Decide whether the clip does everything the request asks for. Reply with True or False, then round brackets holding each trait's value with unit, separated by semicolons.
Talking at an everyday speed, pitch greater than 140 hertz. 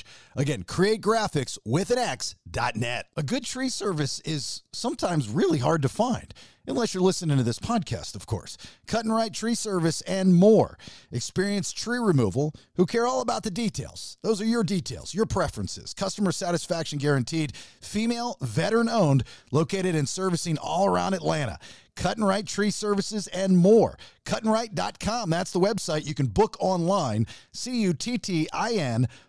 True (150 wpm; 185 Hz)